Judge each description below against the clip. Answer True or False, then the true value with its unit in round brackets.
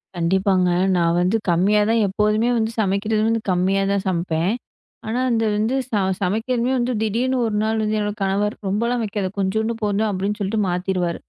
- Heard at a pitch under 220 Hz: True (210 Hz)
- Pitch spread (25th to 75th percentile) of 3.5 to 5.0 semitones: False (2.7 semitones)